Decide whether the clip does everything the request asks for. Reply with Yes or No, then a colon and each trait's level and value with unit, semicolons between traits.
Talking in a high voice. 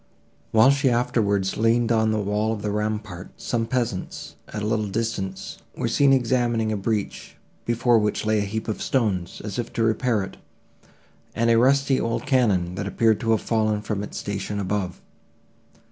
No: low, 110 Hz